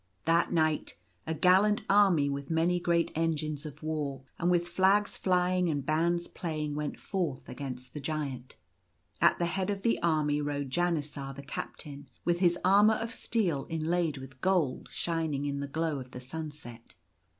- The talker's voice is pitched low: No, medium, 160 Hz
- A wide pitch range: No, average, 3.6 semitones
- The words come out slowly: No, average, 165 wpm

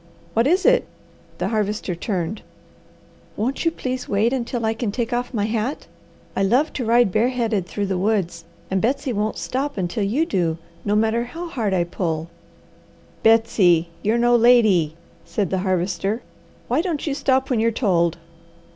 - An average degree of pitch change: Yes, average, 4.4 semitones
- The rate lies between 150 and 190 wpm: Yes, average, 165 wpm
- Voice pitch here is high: Yes, high, 220 Hz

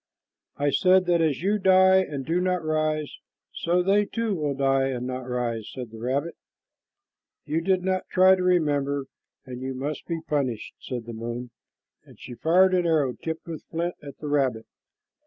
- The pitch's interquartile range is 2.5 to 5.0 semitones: No, wide, 5.5 semitones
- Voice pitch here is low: No, medium, 155 Hz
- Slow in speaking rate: No, average, 180 wpm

